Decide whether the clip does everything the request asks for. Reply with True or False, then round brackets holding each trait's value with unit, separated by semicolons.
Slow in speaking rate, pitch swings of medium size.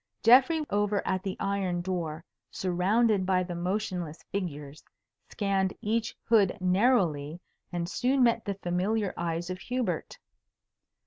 True (125 wpm; 3.6 semitones)